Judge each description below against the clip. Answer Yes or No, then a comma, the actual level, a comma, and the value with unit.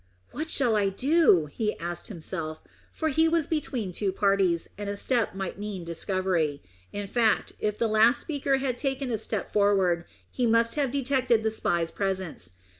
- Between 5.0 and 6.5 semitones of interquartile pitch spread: Yes, wide, 5.5 semitones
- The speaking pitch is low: No, high, 210 Hz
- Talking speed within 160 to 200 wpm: Yes, average, 175 wpm